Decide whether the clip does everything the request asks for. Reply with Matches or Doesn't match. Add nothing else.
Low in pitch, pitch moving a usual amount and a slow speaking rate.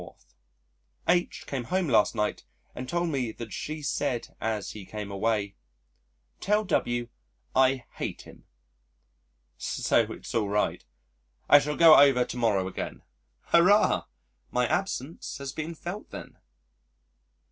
Doesn't match